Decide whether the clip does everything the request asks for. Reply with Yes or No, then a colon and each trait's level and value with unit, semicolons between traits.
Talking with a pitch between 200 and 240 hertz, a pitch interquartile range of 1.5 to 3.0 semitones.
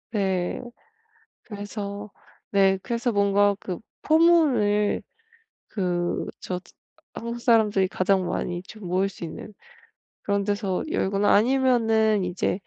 Yes: high, 205 Hz; narrow, 2.6 semitones